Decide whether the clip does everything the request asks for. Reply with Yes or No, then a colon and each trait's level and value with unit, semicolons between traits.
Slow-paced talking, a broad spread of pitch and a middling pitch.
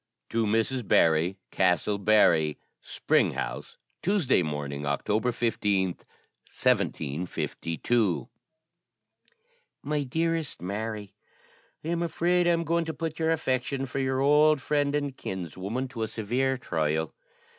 No: slow, 120 wpm; wide, 7.8 semitones; low, 120 Hz